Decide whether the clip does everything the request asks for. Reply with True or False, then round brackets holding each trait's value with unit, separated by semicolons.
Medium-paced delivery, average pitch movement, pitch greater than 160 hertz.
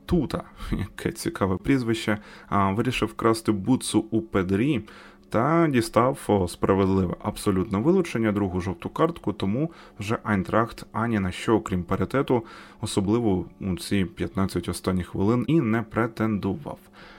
False (120 wpm; 3.3 semitones; 105 Hz)